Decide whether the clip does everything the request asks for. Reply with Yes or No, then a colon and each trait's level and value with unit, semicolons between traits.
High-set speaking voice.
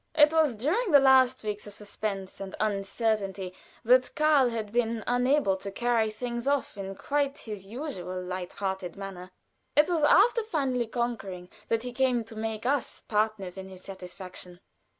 Yes: high, 225 Hz